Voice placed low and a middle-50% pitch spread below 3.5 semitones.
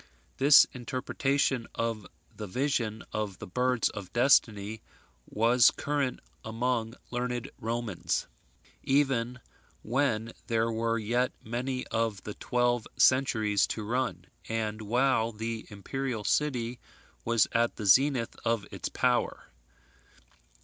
Yes: low, 115 Hz; narrow, 2.5 semitones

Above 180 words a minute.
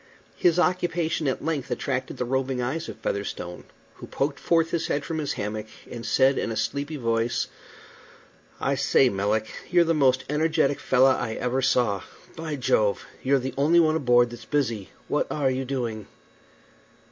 No: average, 170 wpm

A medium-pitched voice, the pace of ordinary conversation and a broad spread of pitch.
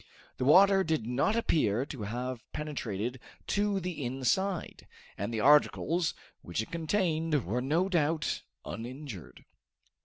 No: medium, 145 Hz; slow, 125 wpm; wide, 5.8 semitones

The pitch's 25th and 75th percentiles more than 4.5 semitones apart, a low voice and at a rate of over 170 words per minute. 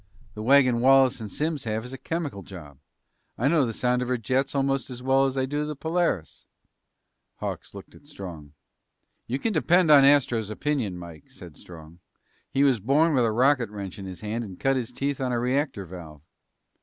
Yes: average, 5.1 semitones; low, 125 Hz; average, 200 wpm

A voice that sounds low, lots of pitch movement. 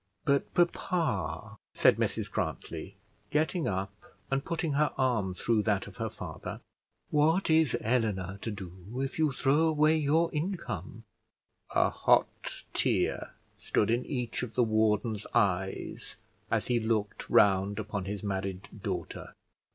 Yes: low, 115 Hz; wide, 6.9 semitones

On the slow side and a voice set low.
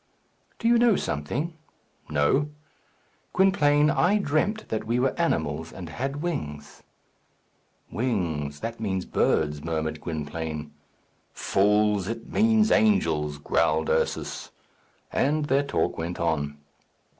Yes: slow, 110 wpm; low, 105 Hz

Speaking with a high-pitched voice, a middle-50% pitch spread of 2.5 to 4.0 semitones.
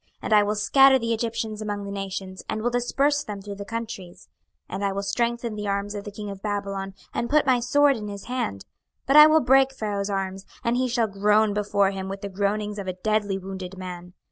Yes: high, 205 Hz; average, 3.0 semitones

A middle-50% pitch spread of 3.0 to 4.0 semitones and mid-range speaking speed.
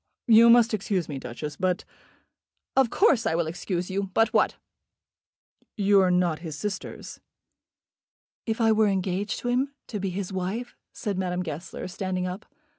Yes: average, 3.5 semitones; average, 170 wpm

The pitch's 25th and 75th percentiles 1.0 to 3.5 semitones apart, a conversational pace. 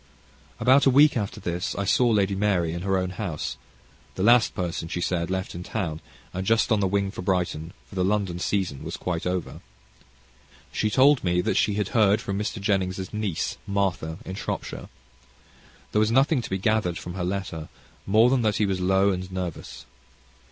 Yes: average, 2.9 semitones; average, 195 wpm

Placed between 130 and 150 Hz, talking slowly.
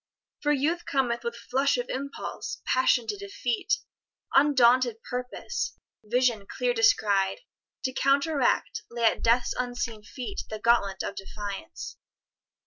No: high, 245 Hz; slow, 125 wpm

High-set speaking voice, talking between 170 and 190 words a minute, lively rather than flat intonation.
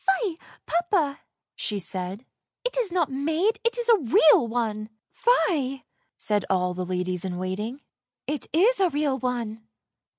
Yes: very high, 260 Hz; average, 185 wpm; wide, 8.5 semitones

